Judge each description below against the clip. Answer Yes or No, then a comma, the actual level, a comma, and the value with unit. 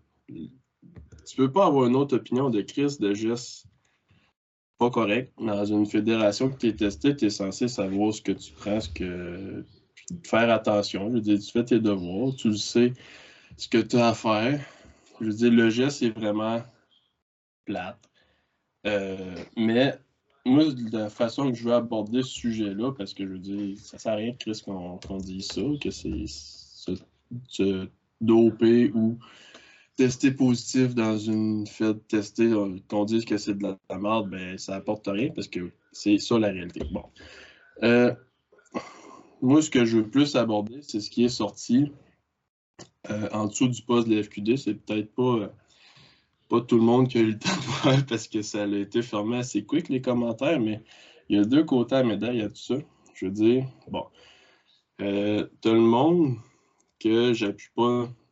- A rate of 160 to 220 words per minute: Yes, average, 190 wpm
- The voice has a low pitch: Yes, low, 110 Hz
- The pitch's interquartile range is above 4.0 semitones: No, average, 3.0 semitones